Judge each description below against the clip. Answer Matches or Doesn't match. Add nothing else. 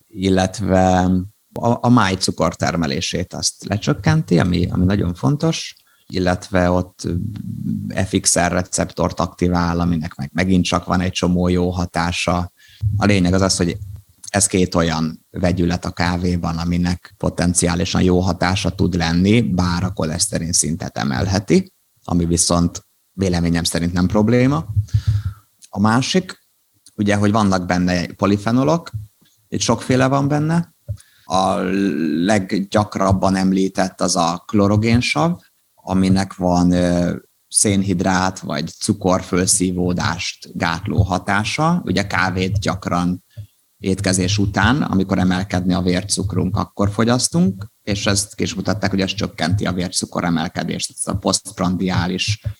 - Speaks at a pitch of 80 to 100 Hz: Matches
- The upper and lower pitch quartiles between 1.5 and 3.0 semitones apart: Matches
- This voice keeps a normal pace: Matches